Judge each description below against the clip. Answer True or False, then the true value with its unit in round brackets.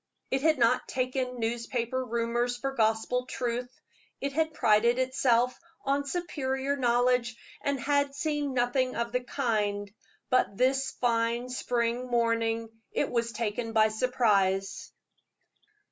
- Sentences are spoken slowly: True (125 wpm)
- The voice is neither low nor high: False (245 Hz)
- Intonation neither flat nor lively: False (2.2 semitones)